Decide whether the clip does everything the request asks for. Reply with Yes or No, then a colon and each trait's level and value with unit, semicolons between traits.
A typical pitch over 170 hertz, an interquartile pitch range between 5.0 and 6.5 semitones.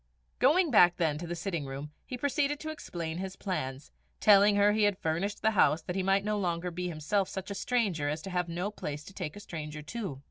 No: medium, 185 Hz; average, 4.4 semitones